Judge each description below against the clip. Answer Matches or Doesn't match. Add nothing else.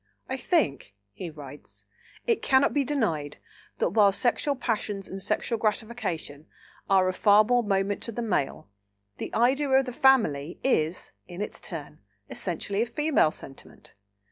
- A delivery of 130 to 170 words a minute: Matches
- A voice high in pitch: Matches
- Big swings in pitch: Matches